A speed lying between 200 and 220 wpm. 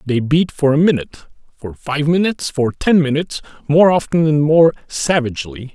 No: average, 165 wpm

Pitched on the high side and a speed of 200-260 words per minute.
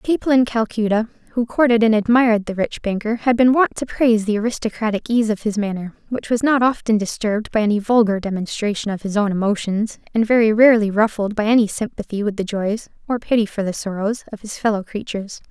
Yes: high, 220 Hz; fast, 205 wpm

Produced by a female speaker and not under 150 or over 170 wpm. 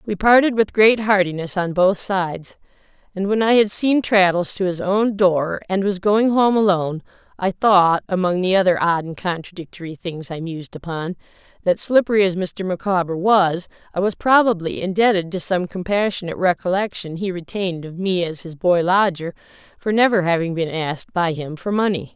No: female; average, 180 wpm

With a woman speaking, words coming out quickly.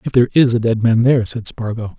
No: male; fast, 270 wpm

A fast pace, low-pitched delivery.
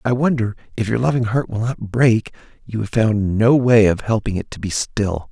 Yes: fast, 225 wpm; low, 110 Hz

